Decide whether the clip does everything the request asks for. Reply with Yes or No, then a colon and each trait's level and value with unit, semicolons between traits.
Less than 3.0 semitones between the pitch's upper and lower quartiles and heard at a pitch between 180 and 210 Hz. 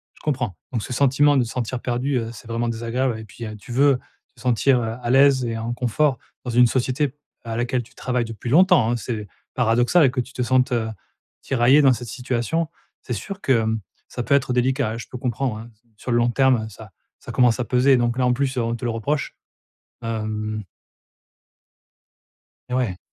No: narrow, 2.4 semitones; low, 120 Hz